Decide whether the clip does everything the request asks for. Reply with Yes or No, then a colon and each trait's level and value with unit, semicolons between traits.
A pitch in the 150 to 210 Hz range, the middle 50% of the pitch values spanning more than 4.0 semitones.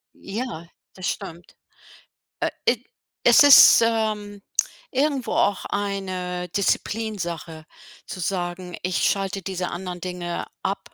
No: high, 190 Hz; average, 2.9 semitones